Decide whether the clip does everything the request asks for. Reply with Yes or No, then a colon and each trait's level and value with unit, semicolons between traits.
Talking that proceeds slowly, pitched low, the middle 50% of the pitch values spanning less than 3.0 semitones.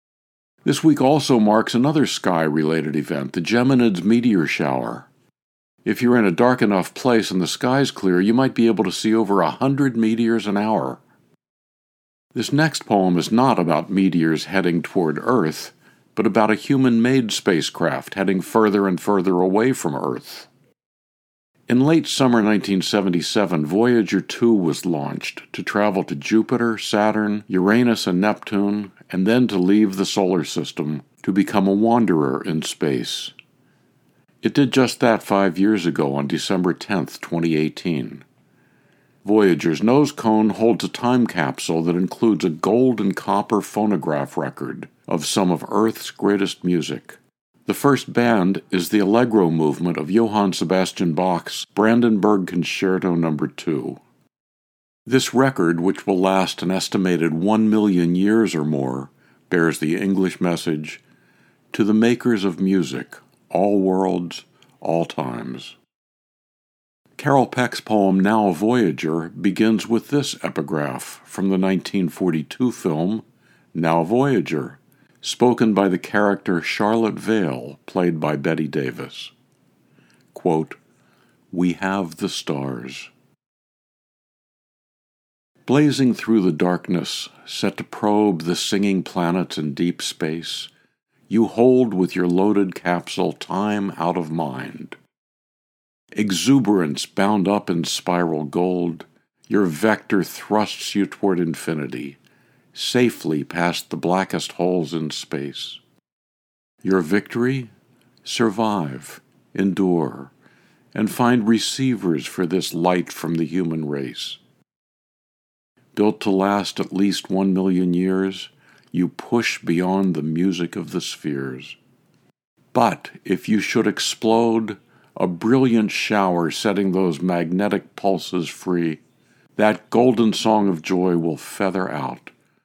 No: slow, 130 wpm; very low, 95 Hz; average, 4.4 semitones